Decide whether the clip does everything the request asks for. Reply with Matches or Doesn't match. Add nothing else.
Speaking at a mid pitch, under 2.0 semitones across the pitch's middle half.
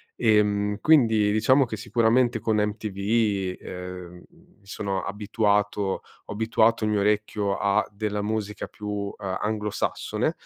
Doesn't match